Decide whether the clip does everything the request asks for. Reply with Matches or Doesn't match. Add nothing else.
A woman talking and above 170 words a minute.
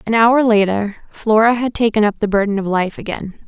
Matches